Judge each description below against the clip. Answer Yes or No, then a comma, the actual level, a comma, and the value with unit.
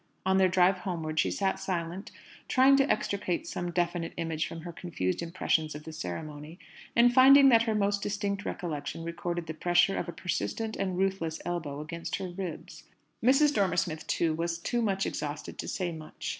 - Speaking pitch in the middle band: Yes, medium, 175 Hz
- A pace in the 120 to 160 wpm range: No, average, 185 wpm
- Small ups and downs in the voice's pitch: No, average, 3.4 semitones